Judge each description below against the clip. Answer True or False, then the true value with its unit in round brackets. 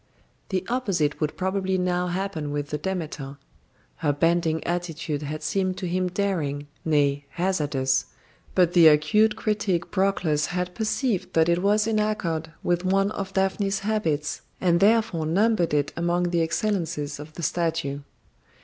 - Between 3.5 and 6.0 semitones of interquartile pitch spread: True (4.1 semitones)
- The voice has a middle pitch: True (175 Hz)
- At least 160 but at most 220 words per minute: False (150 wpm)